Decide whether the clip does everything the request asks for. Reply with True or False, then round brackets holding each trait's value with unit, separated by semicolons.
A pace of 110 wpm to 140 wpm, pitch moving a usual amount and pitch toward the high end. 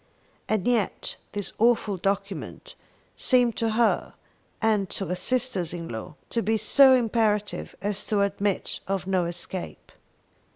True (135 wpm; 3.2 semitones; 205 Hz)